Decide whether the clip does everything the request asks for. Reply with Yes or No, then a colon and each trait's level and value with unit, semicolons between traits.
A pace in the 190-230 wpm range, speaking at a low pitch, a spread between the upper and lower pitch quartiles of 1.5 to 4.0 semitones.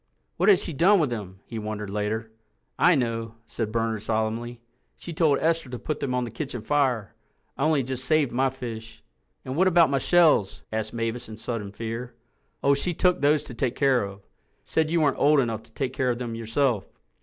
No: average, 200 wpm; low, 125 Hz; average, 4.5 semitones